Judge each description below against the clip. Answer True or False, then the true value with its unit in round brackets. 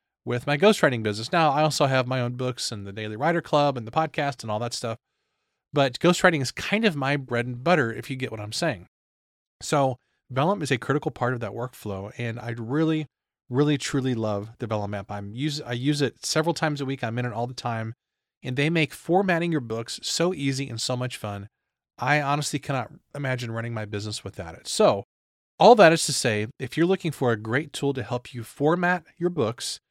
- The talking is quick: True (225 wpm)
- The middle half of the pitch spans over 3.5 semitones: True (4.7 semitones)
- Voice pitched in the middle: False (130 Hz)